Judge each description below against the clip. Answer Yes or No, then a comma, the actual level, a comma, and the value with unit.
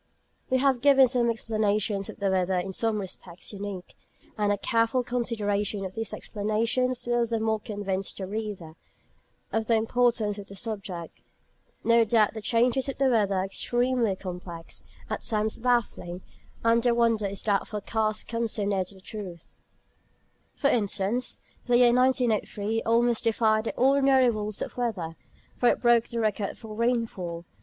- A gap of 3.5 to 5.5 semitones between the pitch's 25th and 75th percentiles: No, average, 3.0 semitones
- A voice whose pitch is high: Yes, high, 220 Hz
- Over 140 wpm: Yes, average, 160 wpm